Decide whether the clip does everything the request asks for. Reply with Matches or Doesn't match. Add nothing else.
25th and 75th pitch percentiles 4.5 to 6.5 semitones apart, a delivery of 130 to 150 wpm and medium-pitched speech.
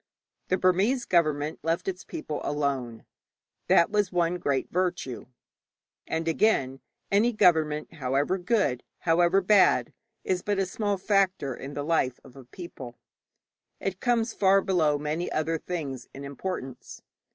Matches